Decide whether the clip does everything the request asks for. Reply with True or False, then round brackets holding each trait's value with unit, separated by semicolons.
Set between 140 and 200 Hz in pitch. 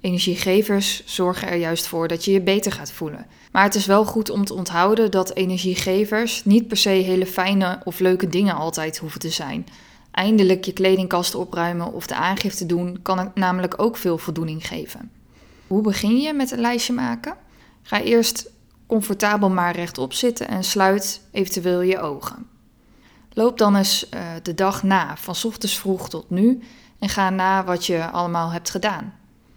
True (190 Hz)